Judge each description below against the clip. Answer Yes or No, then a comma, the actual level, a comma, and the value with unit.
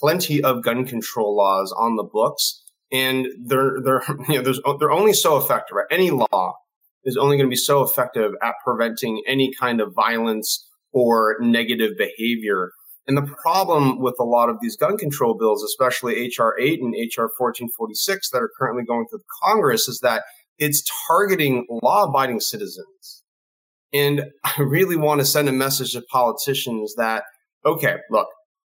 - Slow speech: No, average, 165 wpm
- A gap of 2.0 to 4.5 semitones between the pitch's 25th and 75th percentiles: Yes, average, 4.1 semitones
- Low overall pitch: Yes, low, 130 Hz